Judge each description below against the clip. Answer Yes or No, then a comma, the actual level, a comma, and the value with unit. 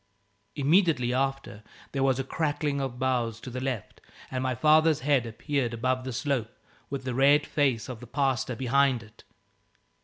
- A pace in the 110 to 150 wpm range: No, average, 165 wpm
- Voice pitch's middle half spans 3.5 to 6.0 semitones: No, narrow, 2.4 semitones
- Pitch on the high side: No, low, 130 Hz